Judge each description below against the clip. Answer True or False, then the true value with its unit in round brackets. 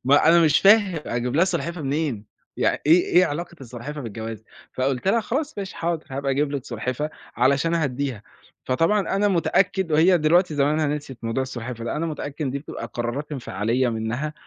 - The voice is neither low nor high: True (145 Hz)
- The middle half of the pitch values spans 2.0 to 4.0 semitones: False (5.0 semitones)